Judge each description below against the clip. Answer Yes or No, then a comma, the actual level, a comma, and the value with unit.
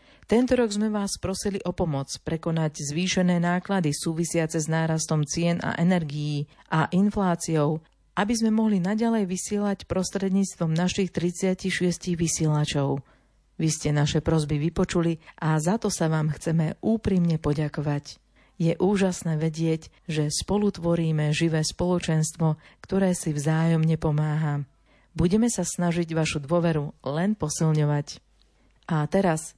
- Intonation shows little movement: No, average, 3.0 semitones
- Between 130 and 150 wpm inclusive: No, average, 120 wpm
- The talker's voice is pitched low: No, medium, 165 Hz